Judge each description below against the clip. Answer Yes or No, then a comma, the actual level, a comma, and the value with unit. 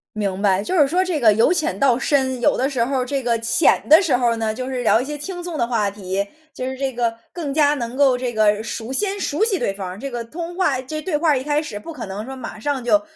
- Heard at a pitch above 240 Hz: Yes, very high, 260 Hz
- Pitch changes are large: No, average, 4.7 semitones